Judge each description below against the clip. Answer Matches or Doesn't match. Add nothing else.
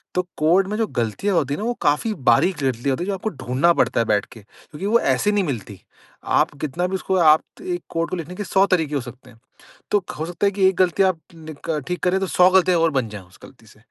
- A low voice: Doesn't match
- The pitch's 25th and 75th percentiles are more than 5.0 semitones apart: Matches